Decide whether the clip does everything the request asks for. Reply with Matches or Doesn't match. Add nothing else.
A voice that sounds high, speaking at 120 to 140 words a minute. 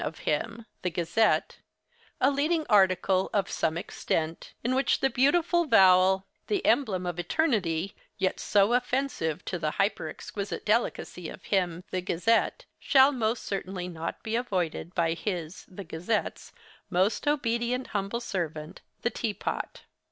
Matches